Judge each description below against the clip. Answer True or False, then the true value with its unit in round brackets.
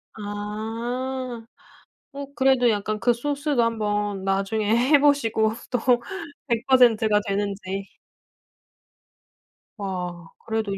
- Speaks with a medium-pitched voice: False (220 Hz)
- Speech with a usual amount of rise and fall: True (3.3 semitones)